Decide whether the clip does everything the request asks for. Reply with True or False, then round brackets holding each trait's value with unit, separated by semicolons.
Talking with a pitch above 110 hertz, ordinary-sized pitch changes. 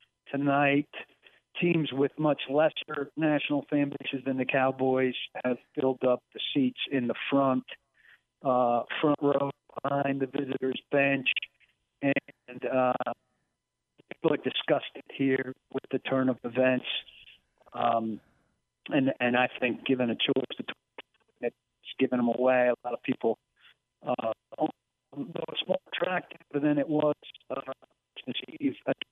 False (135 Hz; 2.2 semitones)